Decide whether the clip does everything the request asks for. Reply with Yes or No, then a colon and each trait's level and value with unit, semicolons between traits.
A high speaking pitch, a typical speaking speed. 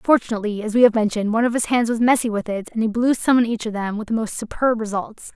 No: high, 225 Hz; fast, 290 wpm